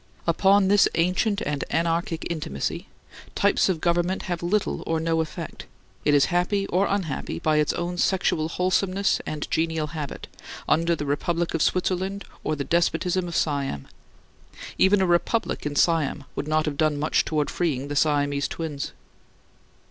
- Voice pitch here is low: No, medium, 165 Hz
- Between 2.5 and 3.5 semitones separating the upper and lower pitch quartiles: Yes, average, 3.2 semitones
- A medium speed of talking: Yes, average, 155 wpm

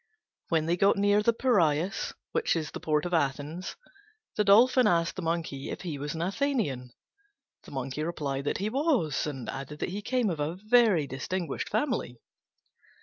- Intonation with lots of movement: Yes, wide, 6.1 semitones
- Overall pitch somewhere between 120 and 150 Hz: No, medium, 170 Hz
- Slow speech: No, average, 175 wpm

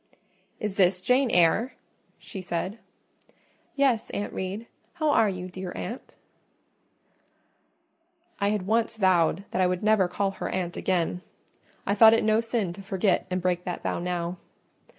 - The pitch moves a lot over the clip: No, average, 3.4 semitones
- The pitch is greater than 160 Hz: Yes, high, 190 Hz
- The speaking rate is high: No, average, 150 wpm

